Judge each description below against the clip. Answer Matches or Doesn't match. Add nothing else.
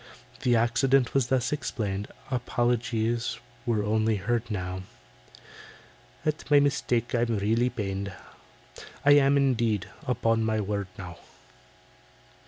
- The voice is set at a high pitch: Doesn't match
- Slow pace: Matches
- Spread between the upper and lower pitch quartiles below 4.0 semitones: Matches